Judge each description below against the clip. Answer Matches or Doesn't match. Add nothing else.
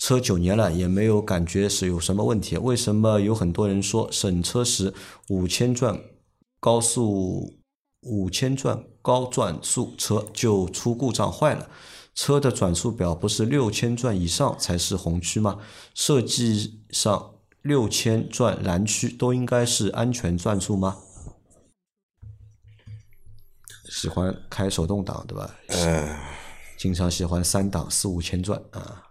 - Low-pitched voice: Matches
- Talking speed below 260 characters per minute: Matches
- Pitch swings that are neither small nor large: Matches